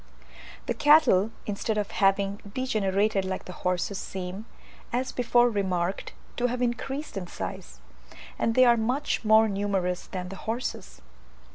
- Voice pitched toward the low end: No, high, 205 Hz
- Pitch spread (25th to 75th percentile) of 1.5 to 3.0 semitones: No, average, 4.0 semitones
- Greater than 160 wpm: No, average, 140 wpm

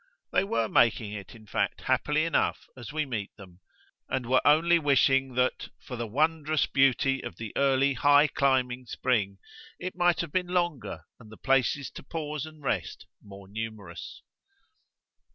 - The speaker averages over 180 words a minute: No, average, 160 wpm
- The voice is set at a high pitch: No, low, 135 Hz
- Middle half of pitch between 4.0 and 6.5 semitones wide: Yes, average, 5.0 semitones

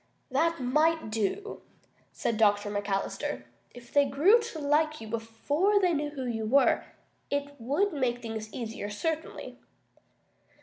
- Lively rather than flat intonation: Yes, wide, 5.9 semitones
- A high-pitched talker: Yes, very high, 275 Hz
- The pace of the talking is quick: No, slow, 135 wpm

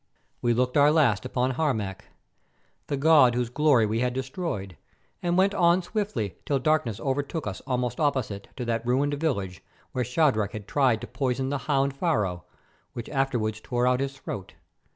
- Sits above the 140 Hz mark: No, low, 130 Hz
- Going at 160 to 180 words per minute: Yes, average, 170 wpm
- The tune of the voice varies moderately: Yes, average, 4.1 semitones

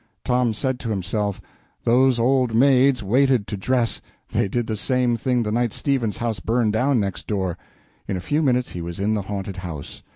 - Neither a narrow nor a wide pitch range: Yes, average, 3.9 semitones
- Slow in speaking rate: No, average, 195 wpm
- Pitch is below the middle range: Yes, low, 115 Hz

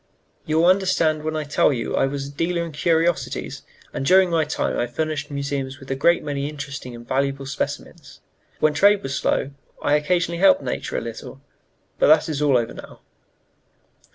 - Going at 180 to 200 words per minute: Yes, average, 185 wpm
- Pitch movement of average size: Yes, average, 3.4 semitones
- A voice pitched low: No, medium, 150 Hz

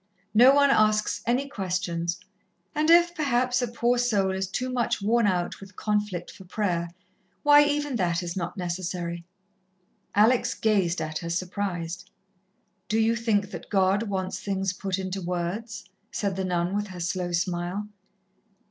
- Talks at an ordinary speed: Yes, average, 155 wpm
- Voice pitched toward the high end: Yes, high, 195 Hz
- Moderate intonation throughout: Yes, average, 4.4 semitones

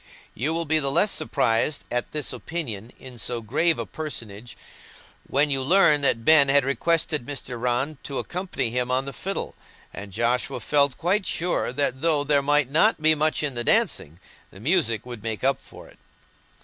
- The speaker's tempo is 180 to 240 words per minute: Yes, average, 185 wpm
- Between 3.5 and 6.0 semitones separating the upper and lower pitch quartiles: Yes, average, 4.4 semitones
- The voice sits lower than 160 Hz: Yes, medium, 140 Hz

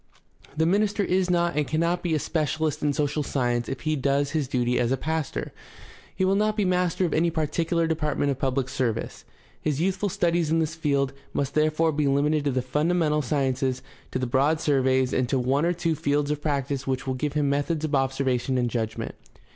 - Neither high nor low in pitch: Yes, medium, 150 Hz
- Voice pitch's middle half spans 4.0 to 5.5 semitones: No, average, 3.5 semitones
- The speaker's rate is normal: No, fast, 210 wpm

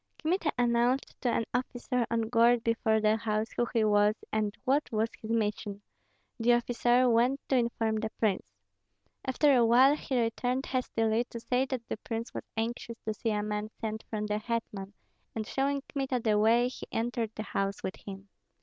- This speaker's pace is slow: No, average, 185 wpm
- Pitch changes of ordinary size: No, narrow, 2.3 semitones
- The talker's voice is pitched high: Yes, high, 230 Hz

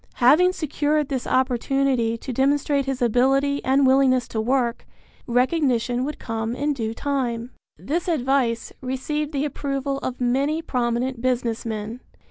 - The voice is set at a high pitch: Yes, very high, 260 Hz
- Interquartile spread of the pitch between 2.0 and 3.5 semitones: Yes, average, 2.7 semitones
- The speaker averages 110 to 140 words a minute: Yes, slow, 135 wpm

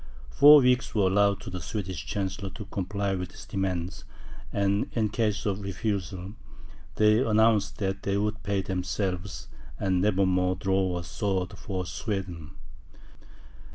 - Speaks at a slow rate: No, average, 145 wpm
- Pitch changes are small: Yes, narrow, 2.1 semitones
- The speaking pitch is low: Yes, very low, 95 Hz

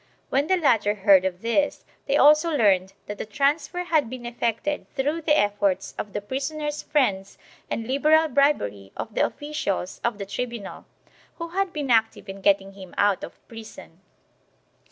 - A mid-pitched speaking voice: No, high, 235 Hz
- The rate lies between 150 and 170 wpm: Yes, average, 165 wpm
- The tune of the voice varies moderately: No, wide, 6.8 semitones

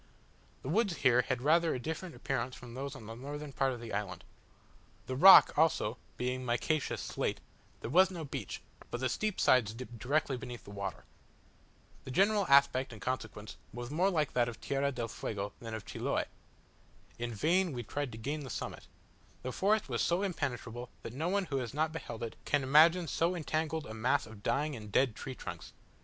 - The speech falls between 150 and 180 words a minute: No, average, 195 wpm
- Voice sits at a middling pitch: No, low, 130 Hz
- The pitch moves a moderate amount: Yes, average, 4.9 semitones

